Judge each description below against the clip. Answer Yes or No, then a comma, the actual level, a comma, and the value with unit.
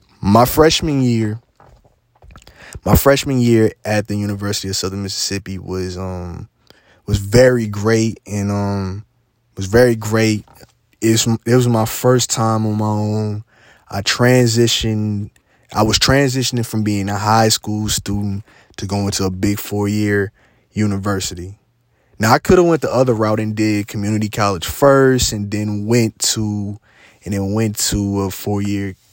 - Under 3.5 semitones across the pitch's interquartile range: Yes, narrow, 2.4 semitones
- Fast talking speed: No, average, 150 wpm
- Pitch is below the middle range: Yes, low, 105 Hz